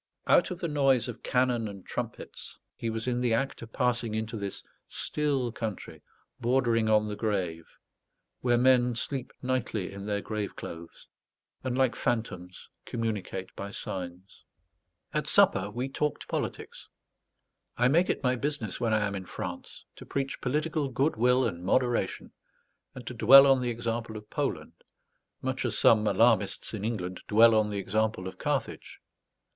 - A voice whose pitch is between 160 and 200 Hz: No, low, 115 Hz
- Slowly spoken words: No, average, 160 wpm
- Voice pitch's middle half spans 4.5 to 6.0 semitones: No, average, 3.5 semitones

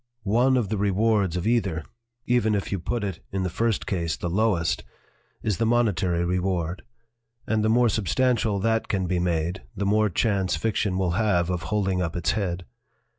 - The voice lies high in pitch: No, low, 100 Hz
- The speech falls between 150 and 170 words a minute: No, average, 180 wpm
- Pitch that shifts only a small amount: No, average, 3.7 semitones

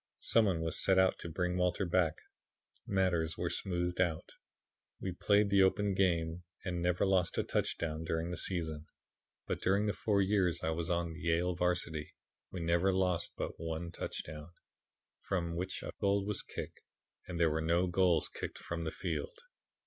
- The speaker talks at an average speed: Yes, average, 175 wpm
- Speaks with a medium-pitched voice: No, very low, 90 Hz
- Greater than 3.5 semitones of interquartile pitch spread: No, narrow, 2.4 semitones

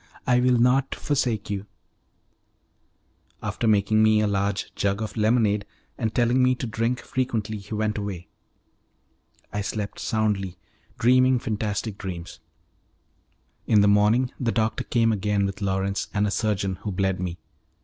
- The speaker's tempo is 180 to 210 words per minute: No, average, 145 wpm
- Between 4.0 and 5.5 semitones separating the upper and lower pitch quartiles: No, narrow, 2.6 semitones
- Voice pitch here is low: Yes, low, 105 Hz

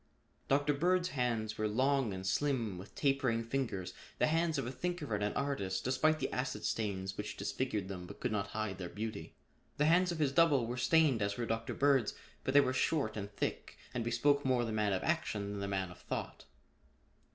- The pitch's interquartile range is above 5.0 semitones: Yes, wide, 5.6 semitones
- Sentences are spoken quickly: Yes, fast, 210 wpm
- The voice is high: No, low, 120 Hz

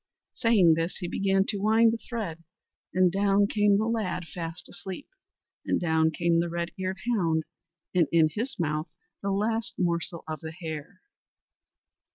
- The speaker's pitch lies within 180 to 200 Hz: Yes, medium, 185 Hz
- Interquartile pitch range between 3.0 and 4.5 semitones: Yes, average, 3.8 semitones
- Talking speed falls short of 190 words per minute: Yes, average, 160 wpm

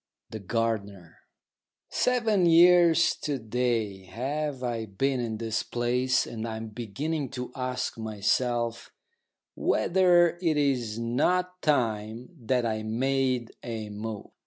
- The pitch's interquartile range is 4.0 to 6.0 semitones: Yes, average, 4.7 semitones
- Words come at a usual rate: No, slow, 120 wpm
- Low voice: Yes, low, 120 Hz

